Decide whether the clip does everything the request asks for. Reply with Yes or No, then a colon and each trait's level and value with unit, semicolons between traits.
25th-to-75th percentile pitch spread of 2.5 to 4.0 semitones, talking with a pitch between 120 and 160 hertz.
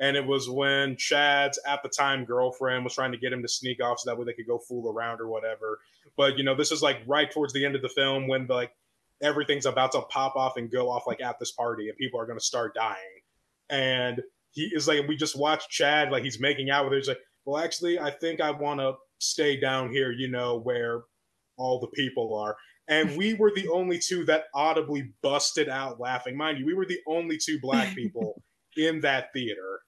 Yes: average, 3.3 semitones; low, 135 Hz